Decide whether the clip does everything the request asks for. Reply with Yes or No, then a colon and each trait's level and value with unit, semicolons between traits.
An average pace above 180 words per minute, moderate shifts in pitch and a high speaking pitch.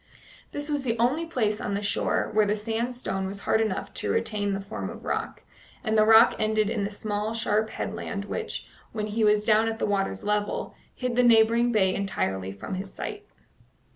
No: average, 200 wpm; narrow, 2.1 semitones; high, 215 Hz